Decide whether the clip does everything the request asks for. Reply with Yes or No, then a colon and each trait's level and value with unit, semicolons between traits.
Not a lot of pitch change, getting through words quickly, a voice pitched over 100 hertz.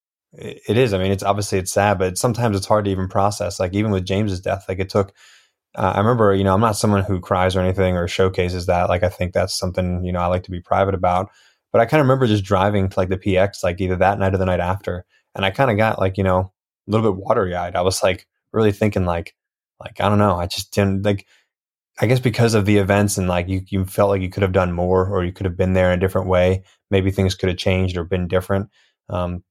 No: narrow, 1.6 semitones; fast, 270 wpm; very low, 95 Hz